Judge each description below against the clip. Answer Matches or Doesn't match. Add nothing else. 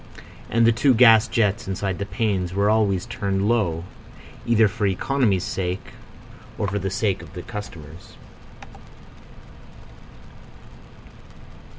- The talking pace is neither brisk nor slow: Doesn't match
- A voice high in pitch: Doesn't match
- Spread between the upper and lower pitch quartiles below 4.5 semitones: Matches